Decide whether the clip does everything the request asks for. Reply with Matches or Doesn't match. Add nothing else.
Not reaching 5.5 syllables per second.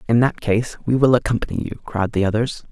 Doesn't match